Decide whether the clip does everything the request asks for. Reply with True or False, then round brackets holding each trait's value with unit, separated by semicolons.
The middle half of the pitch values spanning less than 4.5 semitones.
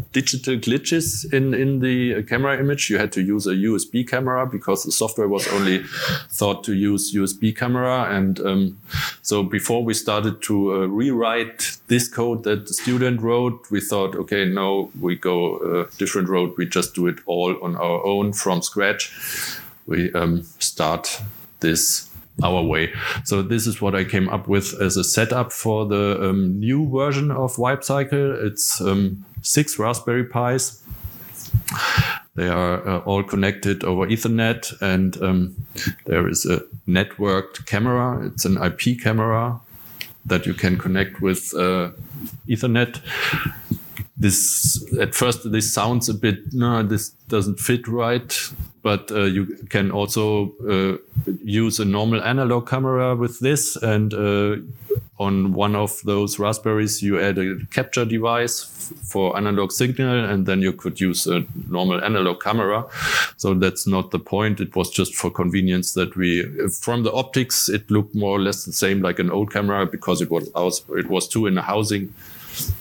True (3.9 semitones)